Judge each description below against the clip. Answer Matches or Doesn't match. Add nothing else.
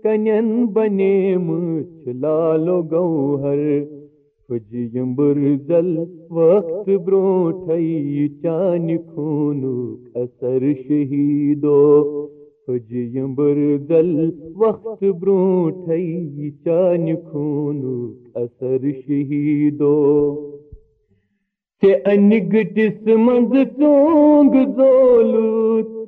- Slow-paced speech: Matches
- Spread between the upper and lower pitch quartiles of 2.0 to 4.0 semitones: Doesn't match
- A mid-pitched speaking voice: Matches